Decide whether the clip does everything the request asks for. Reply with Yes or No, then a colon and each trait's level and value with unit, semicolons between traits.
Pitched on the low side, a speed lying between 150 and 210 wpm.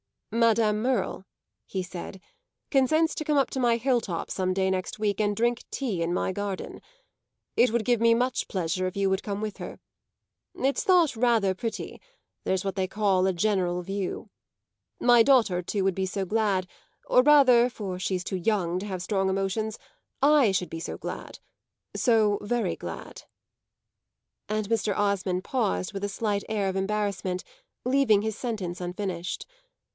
No: high, 205 Hz; average, 170 wpm